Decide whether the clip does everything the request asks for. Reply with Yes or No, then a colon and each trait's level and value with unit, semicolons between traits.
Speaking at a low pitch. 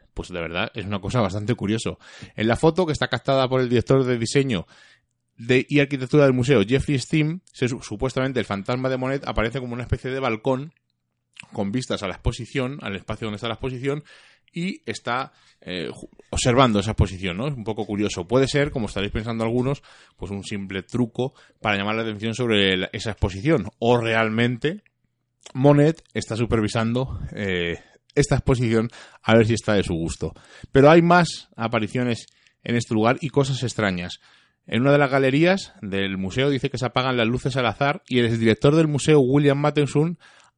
Yes: low, 120 Hz